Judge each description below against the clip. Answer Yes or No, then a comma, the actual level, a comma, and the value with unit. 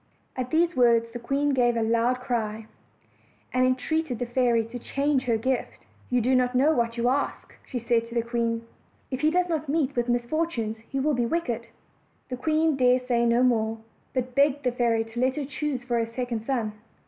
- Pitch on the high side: Yes, very high, 250 Hz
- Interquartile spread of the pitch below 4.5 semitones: Yes, average, 2.7 semitones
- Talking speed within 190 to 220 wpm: Yes, fast, 205 wpm